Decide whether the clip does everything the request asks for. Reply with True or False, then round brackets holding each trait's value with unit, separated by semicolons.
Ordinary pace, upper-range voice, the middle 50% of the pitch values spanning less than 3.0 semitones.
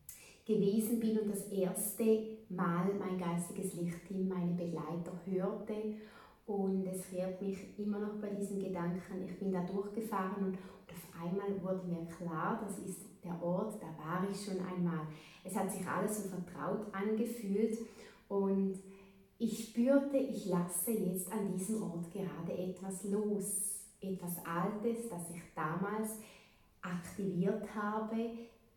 True (140 wpm; 195 Hz; 2.6 semitones)